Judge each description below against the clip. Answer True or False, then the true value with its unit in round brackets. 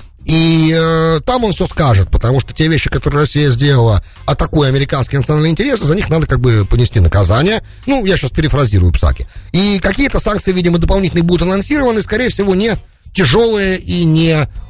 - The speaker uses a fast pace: False (170 wpm)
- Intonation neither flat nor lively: False (6.5 semitones)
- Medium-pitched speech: True (160 Hz)